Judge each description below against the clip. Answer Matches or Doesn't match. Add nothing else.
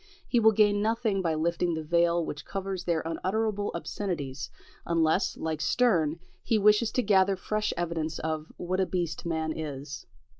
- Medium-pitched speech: Matches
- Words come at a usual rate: Matches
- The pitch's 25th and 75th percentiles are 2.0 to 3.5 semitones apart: Doesn't match